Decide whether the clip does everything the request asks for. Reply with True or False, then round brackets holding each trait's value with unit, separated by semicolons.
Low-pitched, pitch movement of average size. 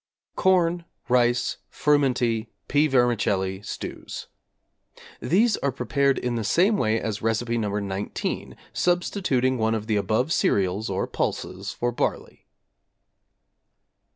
True (120 Hz; 4.8 semitones)